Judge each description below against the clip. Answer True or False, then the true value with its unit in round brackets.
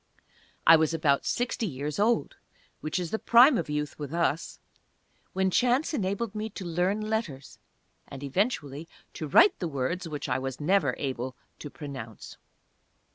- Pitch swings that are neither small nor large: False (6.5 semitones)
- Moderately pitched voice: True (165 Hz)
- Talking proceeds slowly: False (155 wpm)